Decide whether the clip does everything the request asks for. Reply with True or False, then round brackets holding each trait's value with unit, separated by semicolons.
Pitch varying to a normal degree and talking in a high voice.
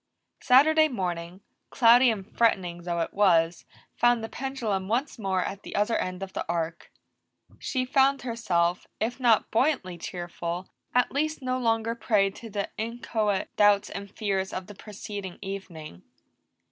True (4.6 semitones; 205 Hz)